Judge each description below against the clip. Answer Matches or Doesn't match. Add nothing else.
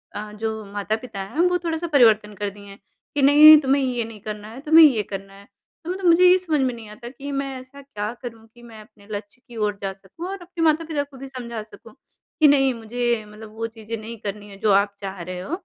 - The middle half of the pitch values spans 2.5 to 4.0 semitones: Doesn't match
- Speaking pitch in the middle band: Doesn't match